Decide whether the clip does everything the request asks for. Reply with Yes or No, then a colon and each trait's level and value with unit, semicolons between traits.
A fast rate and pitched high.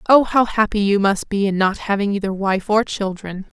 Yes: fast, 215 wpm; high, 200 Hz